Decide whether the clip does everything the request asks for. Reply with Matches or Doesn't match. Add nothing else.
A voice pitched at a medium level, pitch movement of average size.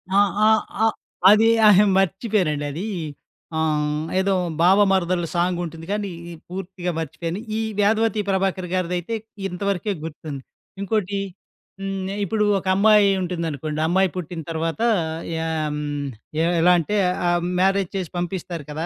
Matches